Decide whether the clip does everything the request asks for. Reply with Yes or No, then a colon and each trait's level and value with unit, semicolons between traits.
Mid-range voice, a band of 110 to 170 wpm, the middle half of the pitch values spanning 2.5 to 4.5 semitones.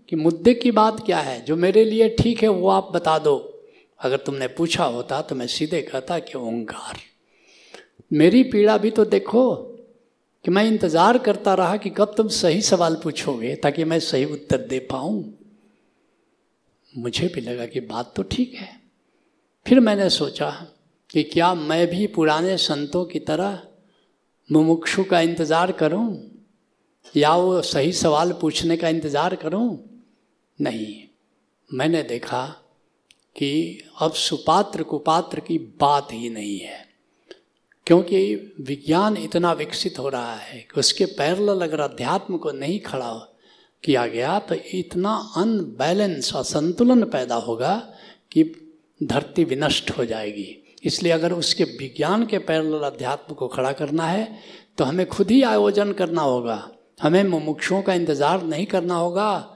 No: medium, 170 Hz; average, 145 wpm; average, 5.2 semitones